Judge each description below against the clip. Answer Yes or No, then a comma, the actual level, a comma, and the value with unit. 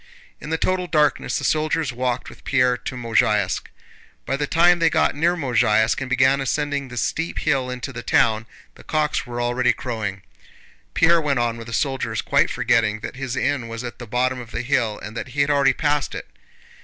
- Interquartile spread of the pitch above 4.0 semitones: No, average, 3.7 semitones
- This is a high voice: No, low, 130 Hz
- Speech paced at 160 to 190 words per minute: No, fast, 205 wpm